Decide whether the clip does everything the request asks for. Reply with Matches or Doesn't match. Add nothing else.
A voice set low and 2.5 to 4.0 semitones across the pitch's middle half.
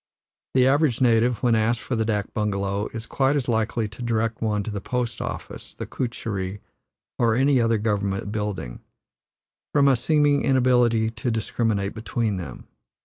Matches